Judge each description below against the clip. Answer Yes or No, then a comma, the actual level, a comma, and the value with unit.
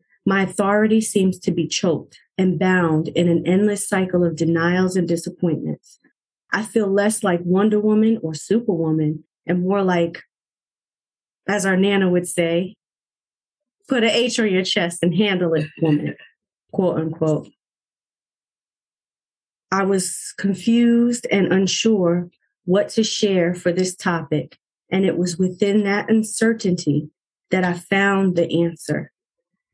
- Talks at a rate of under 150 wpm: Yes, slow, 135 wpm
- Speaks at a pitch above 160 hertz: Yes, medium, 185 Hz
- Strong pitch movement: No, average, 3.2 semitones